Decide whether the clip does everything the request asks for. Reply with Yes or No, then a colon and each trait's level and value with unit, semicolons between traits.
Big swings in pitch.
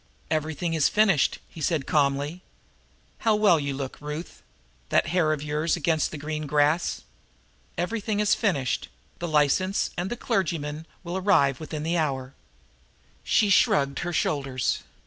No: average, 3.5 semitones